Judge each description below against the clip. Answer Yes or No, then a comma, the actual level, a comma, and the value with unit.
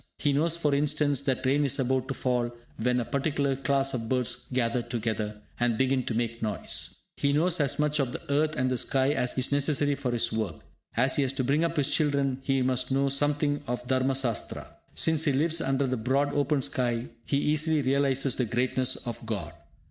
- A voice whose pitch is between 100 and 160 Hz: Yes, low, 135 Hz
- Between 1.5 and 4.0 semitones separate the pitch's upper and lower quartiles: Yes, narrow, 2.5 semitones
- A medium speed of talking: No, fast, 210 wpm